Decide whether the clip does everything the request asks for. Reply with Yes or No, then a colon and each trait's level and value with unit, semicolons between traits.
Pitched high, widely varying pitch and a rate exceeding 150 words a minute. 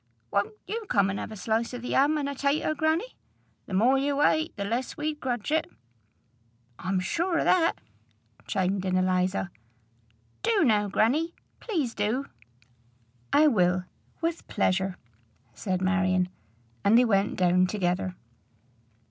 No: high, 225 Hz; wide, 8.1 semitones; average, 145 wpm